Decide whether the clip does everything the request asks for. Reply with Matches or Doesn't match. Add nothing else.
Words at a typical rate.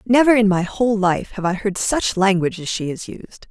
Doesn't match